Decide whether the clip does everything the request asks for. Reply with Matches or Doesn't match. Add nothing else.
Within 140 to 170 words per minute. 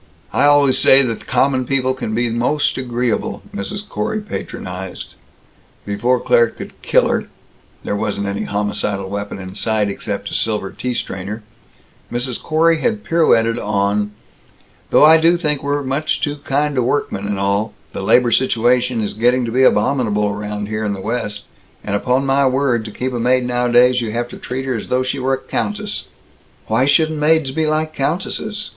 Doesn't match